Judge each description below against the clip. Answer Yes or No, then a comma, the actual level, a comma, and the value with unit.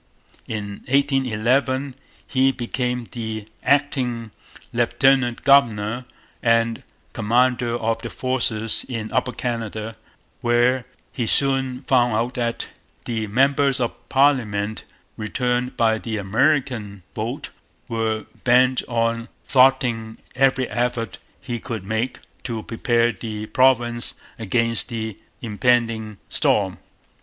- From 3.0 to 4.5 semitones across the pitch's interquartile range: No, narrow, 2.5 semitones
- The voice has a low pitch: Yes, low, 120 Hz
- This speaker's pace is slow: Yes, slow, 105 wpm